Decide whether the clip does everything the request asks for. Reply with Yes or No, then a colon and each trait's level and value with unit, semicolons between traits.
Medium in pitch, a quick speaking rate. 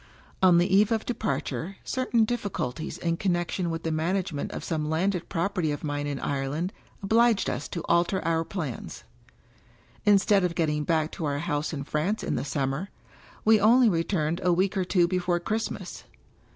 No: medium, 175 Hz; average, 180 wpm